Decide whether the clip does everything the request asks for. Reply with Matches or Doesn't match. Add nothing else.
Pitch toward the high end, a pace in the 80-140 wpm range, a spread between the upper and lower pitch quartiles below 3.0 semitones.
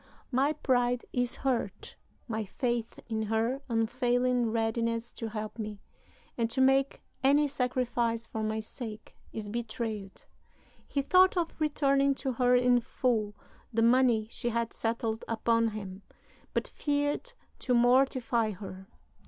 Matches